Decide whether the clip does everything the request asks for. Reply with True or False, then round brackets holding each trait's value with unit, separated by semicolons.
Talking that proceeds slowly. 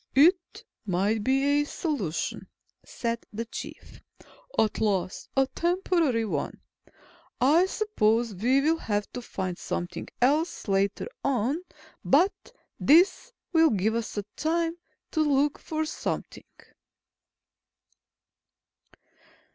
True (105 wpm)